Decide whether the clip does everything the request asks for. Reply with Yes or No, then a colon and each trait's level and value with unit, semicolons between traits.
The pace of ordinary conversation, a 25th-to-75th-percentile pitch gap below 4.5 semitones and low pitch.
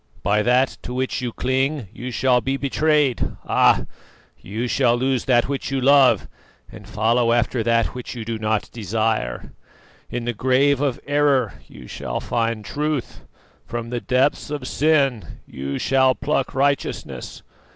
Yes: average, 150 wpm; average, 2.8 semitones; low, 125 Hz